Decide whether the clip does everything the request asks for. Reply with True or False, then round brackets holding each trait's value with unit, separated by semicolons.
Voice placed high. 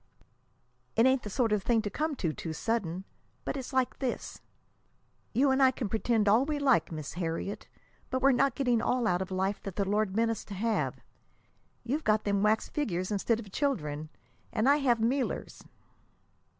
True (225 Hz)